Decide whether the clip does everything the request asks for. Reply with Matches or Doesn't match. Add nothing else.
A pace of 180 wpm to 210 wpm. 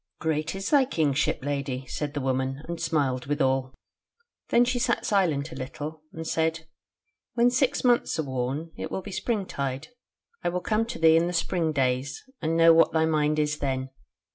Matches